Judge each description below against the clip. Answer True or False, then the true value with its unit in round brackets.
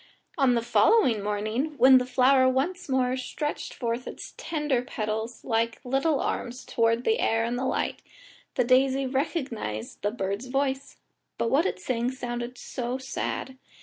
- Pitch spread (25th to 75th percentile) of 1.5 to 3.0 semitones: True (2.6 semitones)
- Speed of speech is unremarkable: True (150 wpm)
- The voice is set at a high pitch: True (255 Hz)